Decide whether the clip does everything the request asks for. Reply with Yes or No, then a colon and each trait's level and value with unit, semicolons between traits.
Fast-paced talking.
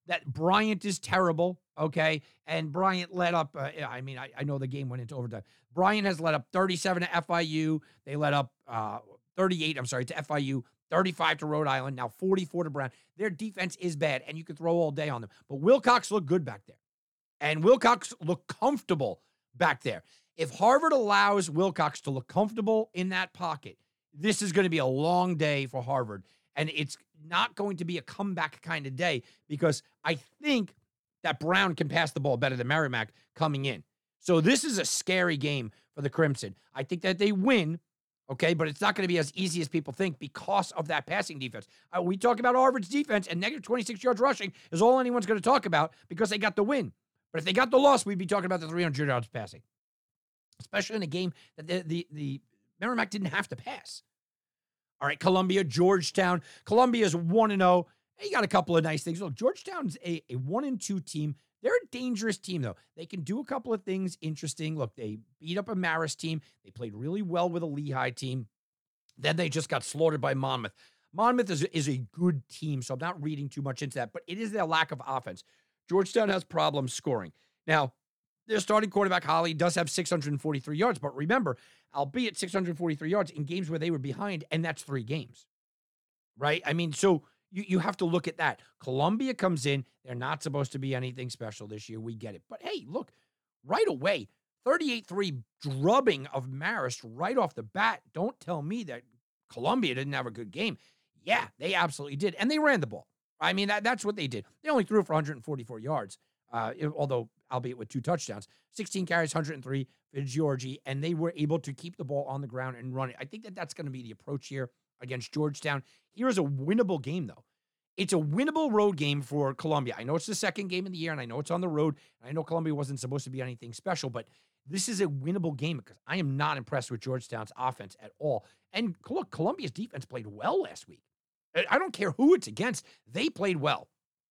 Yes: fast, 215 wpm